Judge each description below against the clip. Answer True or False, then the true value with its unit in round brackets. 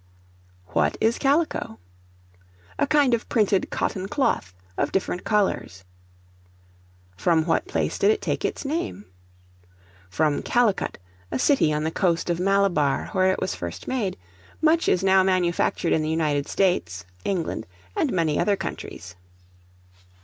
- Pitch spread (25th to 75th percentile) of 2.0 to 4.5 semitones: False (5.5 semitones)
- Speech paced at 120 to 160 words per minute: True (140 wpm)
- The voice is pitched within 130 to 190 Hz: True (185 Hz)